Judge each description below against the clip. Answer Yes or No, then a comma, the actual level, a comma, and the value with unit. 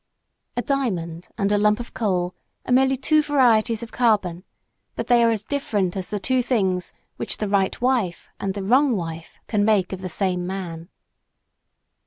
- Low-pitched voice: No, high, 205 Hz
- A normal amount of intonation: Yes, average, 4.8 semitones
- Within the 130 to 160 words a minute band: No, average, 180 wpm